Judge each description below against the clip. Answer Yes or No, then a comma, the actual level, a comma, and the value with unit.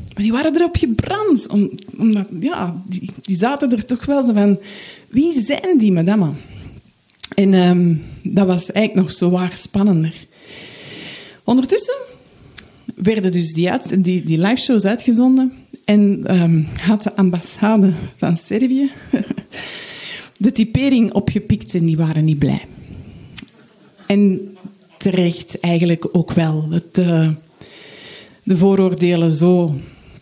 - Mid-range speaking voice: No, high, 195 Hz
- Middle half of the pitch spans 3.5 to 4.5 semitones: Yes, average, 4.2 semitones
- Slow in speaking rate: Yes, slow, 120 wpm